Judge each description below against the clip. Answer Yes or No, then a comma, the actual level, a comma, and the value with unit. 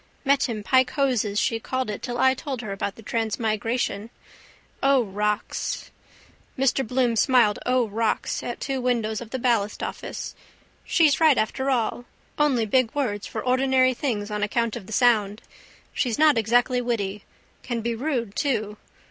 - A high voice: Yes, high, 235 Hz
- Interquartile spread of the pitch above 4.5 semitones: No, average, 3.3 semitones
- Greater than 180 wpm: No, average, 155 wpm